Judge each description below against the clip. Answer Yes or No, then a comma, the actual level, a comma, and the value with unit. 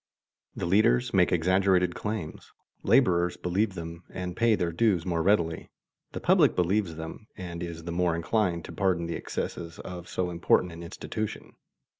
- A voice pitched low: Yes, very low, 90 Hz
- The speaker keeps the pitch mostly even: Yes, narrow, 2.3 semitones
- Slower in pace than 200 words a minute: Yes, average, 160 wpm